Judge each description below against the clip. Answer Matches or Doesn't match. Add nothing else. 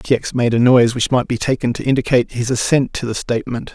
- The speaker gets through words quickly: Matches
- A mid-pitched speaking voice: Doesn't match